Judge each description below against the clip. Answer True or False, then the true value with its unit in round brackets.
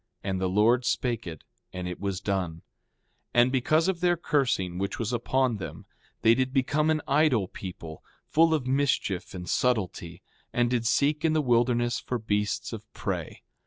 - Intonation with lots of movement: True (5.9 semitones)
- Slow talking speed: False (175 wpm)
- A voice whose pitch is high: False (120 Hz)